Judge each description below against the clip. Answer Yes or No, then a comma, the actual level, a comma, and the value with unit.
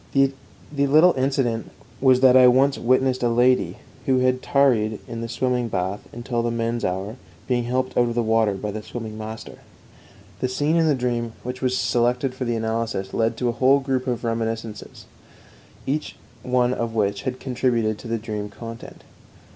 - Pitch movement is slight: Yes, narrow, 2.2 semitones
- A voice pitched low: Yes, low, 120 Hz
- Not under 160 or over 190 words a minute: Yes, average, 180 wpm